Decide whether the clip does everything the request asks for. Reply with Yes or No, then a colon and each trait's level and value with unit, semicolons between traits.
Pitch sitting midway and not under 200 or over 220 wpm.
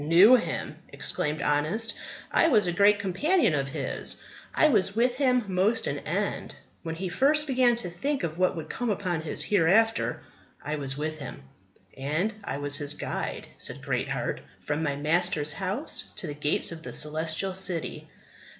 No: medium, 180 Hz; average, 170 wpm